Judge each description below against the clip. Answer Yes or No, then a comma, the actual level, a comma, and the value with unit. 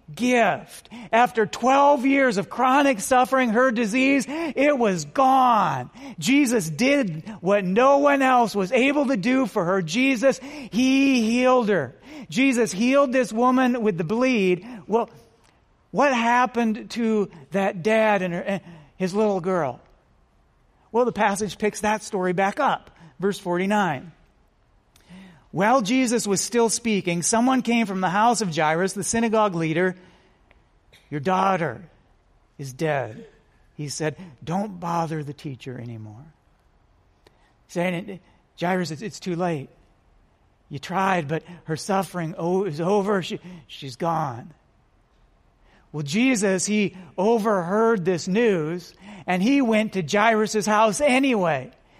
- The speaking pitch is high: Yes, high, 205 Hz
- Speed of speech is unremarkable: No, slow, 130 wpm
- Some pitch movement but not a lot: No, wide, 5.8 semitones